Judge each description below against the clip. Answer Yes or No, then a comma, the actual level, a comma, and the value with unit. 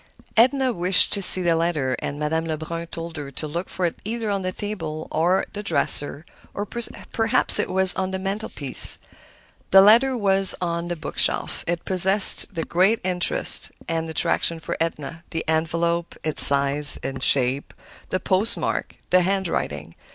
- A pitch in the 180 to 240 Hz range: No, medium, 170 Hz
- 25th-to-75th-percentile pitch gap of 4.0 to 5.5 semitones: No, average, 3.3 semitones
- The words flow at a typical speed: Yes, average, 165 wpm